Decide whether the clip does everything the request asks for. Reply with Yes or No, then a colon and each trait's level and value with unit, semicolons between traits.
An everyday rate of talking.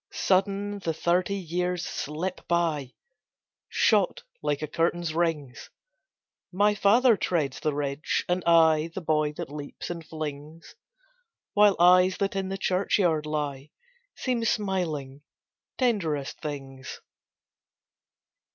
No: slow, 115 wpm